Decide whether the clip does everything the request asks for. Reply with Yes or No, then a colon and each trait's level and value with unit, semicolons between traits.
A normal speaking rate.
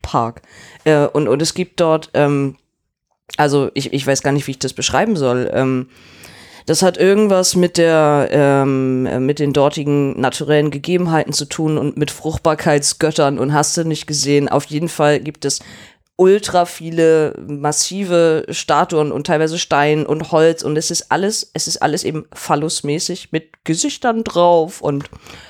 Yes: average, 160 wpm